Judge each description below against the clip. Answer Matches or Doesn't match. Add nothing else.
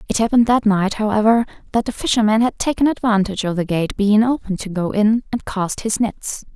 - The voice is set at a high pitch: Matches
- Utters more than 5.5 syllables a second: Matches